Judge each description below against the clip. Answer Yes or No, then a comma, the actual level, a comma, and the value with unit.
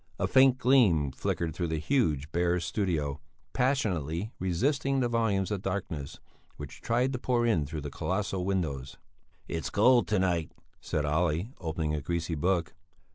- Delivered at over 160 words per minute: No, average, 155 wpm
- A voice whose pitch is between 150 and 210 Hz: No, very low, 90 Hz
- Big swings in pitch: Yes, wide, 6.4 semitones